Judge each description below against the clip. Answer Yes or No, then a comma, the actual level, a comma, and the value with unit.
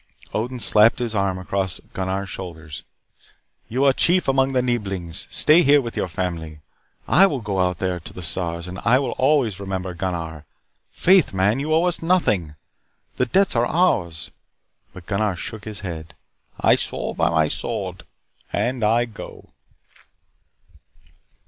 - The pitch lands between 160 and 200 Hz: No, low, 100 Hz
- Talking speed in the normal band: Yes, average, 155 wpm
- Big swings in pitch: Yes, wide, 6.2 semitones